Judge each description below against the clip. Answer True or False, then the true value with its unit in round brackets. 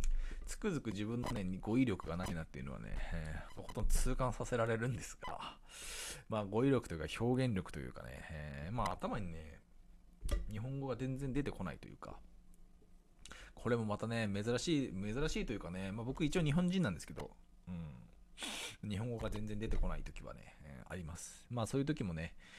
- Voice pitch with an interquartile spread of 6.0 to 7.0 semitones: True (6.6 semitones)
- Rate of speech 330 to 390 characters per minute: True (360 characters per minute)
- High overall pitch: False (105 Hz)